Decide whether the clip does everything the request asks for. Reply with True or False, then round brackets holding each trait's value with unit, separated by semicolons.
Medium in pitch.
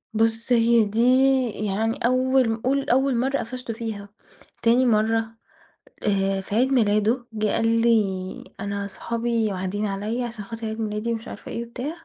False (225 Hz)